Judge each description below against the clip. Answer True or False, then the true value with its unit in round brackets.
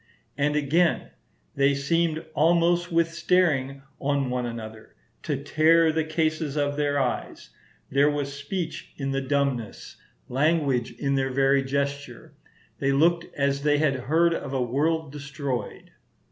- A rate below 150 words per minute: True (140 wpm)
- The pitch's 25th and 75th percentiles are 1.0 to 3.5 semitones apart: True (2.8 semitones)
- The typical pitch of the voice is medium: True (145 Hz)